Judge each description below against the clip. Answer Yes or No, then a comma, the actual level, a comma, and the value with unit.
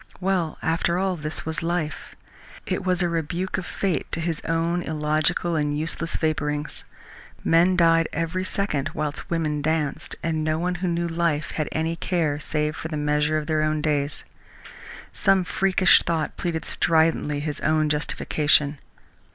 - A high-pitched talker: No, medium, 160 Hz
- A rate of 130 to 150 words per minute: No, average, 160 wpm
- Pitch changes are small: Yes, narrow, 2.1 semitones